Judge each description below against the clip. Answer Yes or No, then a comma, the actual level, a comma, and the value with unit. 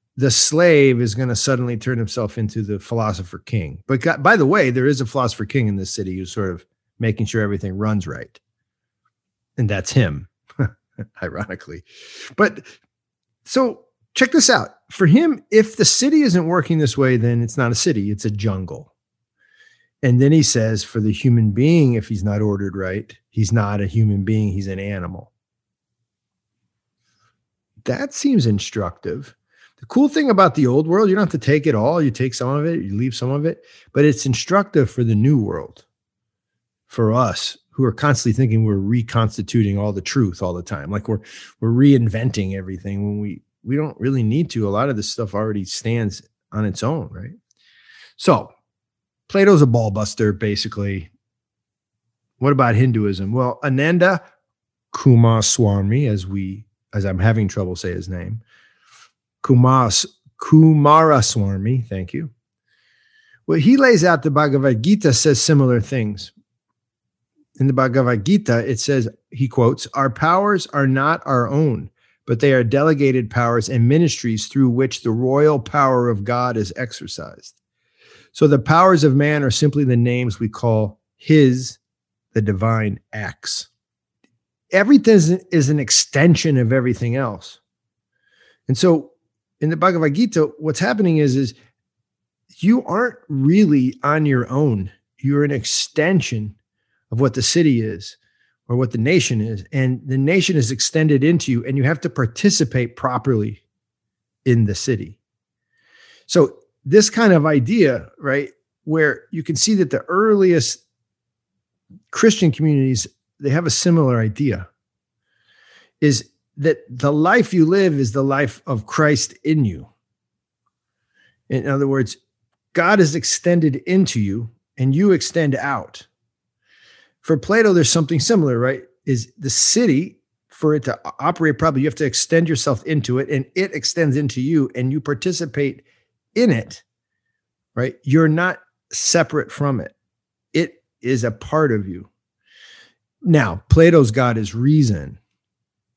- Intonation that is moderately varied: No, wide, 5.8 semitones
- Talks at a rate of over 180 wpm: No, average, 155 wpm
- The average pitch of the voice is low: Yes, low, 130 Hz